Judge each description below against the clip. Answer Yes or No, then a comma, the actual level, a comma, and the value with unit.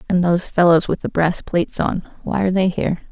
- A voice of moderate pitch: Yes, medium, 180 Hz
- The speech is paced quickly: Yes, fast, 230 wpm